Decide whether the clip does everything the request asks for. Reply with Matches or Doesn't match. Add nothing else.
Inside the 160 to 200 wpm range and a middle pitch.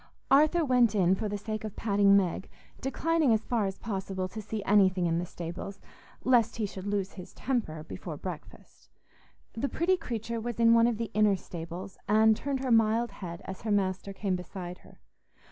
Doesn't match